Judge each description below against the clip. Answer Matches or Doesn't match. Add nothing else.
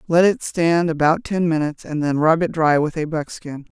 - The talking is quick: Matches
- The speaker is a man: Doesn't match